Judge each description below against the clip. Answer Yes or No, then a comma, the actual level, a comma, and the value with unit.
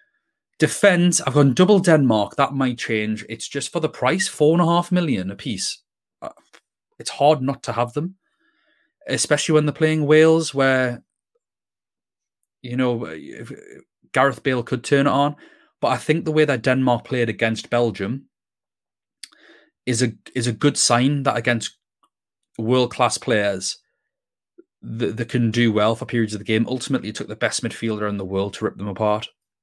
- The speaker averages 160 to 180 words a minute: Yes, average, 170 wpm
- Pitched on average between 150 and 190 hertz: No, low, 130 Hz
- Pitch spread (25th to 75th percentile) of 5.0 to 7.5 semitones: Yes, average, 5.3 semitones